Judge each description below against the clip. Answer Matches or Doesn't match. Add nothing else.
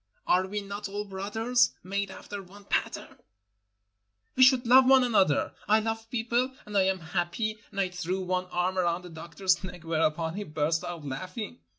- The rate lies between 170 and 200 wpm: Matches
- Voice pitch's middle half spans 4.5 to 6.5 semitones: Doesn't match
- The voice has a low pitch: Doesn't match